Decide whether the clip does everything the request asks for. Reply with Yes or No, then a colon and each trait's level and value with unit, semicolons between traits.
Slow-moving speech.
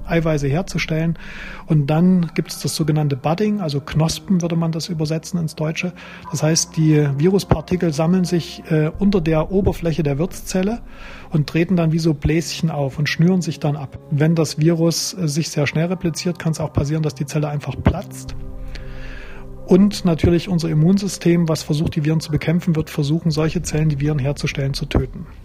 No: average, 175 wpm